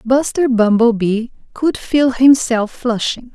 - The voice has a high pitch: Yes, high, 240 Hz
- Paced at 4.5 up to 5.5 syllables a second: No, 3.6 syllables/s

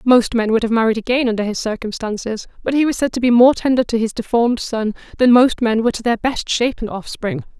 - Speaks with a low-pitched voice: No, high, 235 Hz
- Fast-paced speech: Yes, fast, 235 wpm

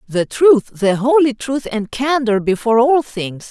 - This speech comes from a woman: Yes, female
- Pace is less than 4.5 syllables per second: Yes, 4.2 syllables/s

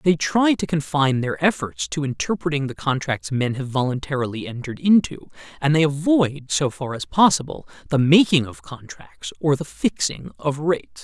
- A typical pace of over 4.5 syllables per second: Yes, 5.1 syllables/s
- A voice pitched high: No, medium, 145 Hz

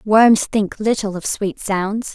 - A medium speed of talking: Yes, average, 170 wpm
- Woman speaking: Yes, female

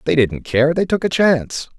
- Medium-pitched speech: Yes, medium, 145 Hz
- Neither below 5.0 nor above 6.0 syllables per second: Yes, 5.1 syllables/s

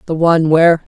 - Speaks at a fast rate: No, average, 190 wpm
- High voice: No, medium, 165 Hz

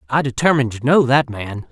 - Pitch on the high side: No, low, 130 Hz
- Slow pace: No, fast, 210 wpm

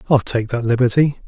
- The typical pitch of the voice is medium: No, low, 125 Hz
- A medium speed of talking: Yes, average, 190 wpm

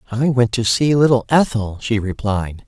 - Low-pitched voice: Yes, low, 120 Hz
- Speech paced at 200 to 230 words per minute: No, average, 180 wpm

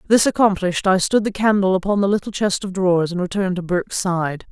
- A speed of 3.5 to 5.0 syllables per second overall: No, 6.3 syllables/s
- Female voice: Yes, female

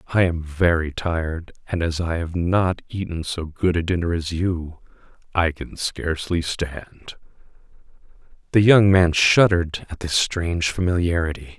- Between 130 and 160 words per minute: Yes, average, 145 wpm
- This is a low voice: Yes, very low, 85 Hz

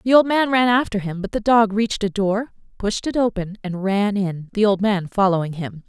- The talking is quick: Yes, fast, 235 wpm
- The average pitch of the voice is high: Yes, high, 205 Hz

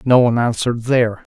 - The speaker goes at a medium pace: Yes, average, 180 wpm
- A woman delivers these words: No, male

